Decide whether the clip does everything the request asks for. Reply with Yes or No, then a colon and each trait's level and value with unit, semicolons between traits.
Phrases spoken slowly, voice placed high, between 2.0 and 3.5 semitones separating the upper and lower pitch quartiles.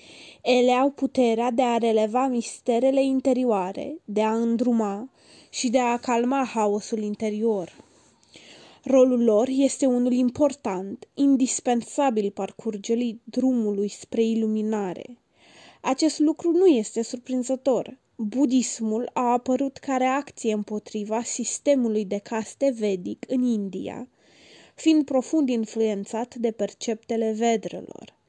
Yes: slow, 105 wpm; high, 240 Hz; average, 3.0 semitones